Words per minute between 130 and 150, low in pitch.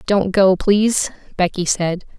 No: slow, 135 wpm; high, 190 Hz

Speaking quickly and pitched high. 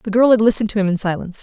Yes: fast, 335 wpm; high, 210 Hz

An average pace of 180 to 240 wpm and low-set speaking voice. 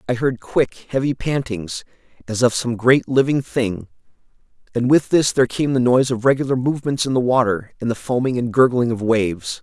Yes: average, 195 wpm; low, 125 Hz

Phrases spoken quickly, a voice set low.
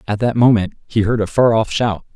Yes: fast, 250 wpm; low, 110 Hz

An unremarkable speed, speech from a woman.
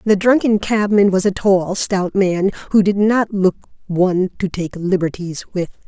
Yes: average, 175 wpm; female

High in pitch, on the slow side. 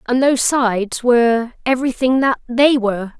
Yes: high, 245 Hz; slow, 130 wpm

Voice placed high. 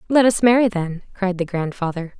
Yes: high, 195 Hz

